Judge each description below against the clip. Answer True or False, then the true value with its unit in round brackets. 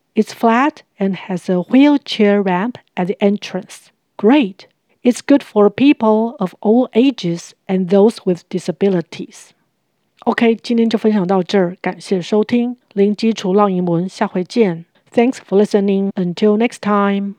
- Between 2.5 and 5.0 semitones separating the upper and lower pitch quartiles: True (3.5 semitones)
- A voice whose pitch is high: True (205 Hz)